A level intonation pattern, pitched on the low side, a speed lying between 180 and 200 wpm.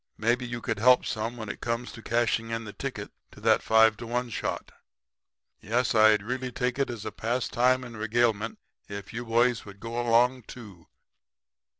Yes: narrow, 1.8 semitones; low, 115 Hz; average, 185 wpm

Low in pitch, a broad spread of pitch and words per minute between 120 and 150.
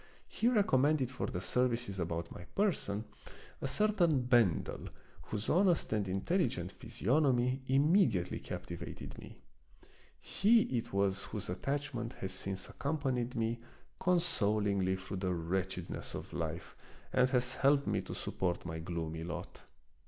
Yes: low, 120 Hz; wide, 7.0 semitones; slow, 135 wpm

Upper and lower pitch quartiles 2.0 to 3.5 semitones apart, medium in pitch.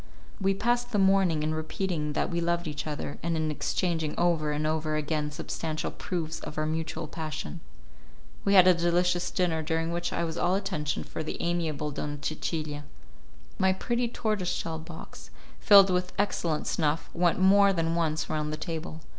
Yes: average, 2.8 semitones; medium, 165 Hz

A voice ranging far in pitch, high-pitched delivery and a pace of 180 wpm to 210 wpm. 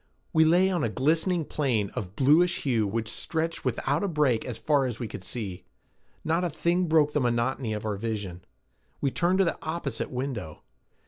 No: wide, 6.4 semitones; low, 135 Hz; average, 190 wpm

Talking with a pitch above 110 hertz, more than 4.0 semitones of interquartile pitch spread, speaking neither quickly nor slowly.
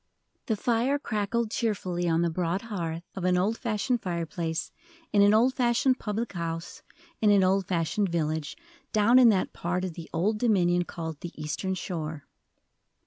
Yes: medium, 185 Hz; average, 4.4 semitones; average, 165 wpm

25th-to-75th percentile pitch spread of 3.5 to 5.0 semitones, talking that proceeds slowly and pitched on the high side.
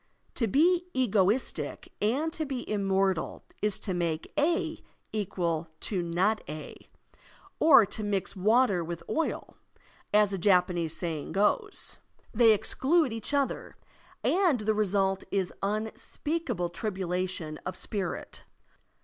No: wide, 5.5 semitones; slow, 120 wpm; high, 205 Hz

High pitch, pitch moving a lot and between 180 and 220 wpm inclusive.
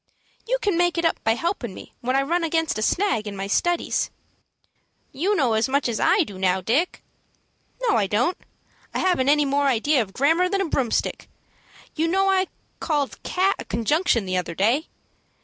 Yes: very high, 285 Hz; wide, 7.7 semitones; average, 190 wpm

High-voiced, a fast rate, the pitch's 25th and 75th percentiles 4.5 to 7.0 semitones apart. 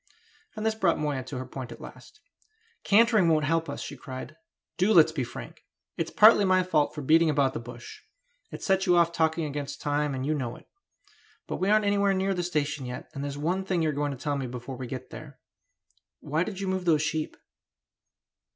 No: medium, 155 Hz; fast, 215 wpm; average, 5.0 semitones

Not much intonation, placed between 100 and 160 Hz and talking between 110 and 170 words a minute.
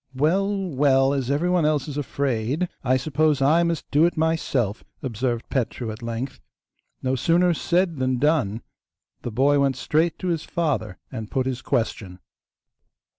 No: average, 4.2 semitones; medium, 140 Hz; average, 155 wpm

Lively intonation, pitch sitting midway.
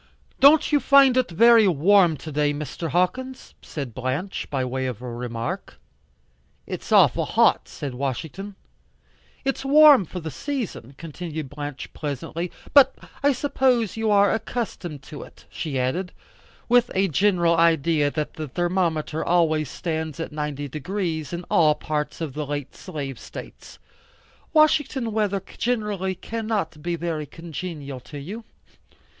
Yes: wide, 6.1 semitones; medium, 170 Hz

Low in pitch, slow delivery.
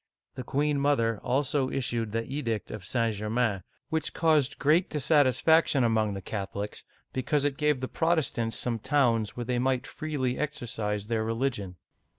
No: low, 125 Hz; average, 155 wpm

